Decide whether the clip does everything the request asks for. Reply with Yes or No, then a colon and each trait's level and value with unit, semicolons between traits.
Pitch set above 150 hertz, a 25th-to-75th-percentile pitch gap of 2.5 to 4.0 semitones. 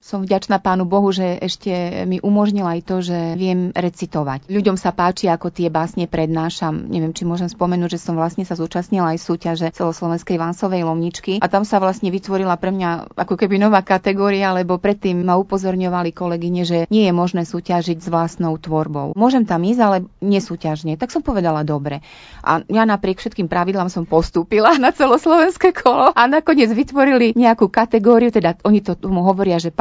Yes: medium, 185 Hz; average, 2.9 semitones